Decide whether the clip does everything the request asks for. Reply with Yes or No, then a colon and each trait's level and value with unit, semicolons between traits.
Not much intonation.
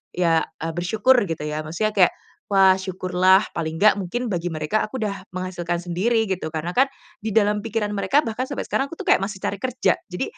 No: average, 3.7 semitones